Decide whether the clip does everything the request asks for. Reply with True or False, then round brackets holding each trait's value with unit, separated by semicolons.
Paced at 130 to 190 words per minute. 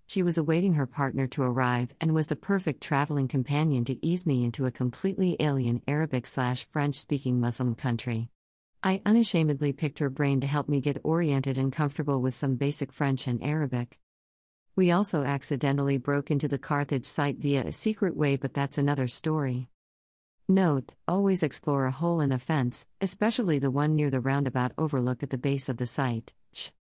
True (180 wpm)